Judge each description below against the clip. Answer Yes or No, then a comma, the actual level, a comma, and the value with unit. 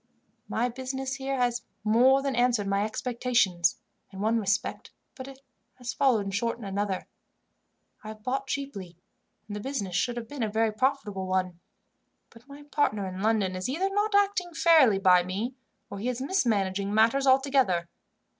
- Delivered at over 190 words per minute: No, average, 165 wpm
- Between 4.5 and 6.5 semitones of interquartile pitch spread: Yes, average, 5.1 semitones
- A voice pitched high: Yes, high, 230 Hz